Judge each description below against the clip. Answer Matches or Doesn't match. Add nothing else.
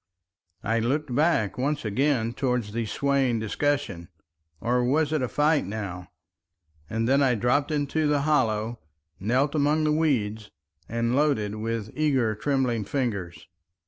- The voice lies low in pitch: Matches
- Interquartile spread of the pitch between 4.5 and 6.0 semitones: Matches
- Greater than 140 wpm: Doesn't match